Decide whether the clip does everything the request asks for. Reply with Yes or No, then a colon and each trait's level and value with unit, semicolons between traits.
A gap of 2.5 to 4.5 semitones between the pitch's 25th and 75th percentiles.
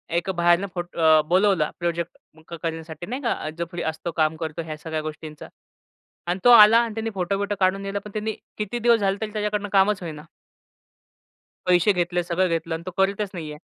Yes: average, 3.9 semitones